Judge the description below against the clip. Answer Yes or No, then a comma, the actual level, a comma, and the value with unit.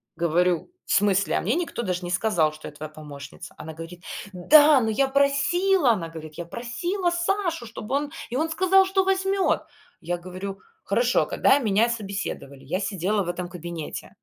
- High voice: Yes, high, 210 Hz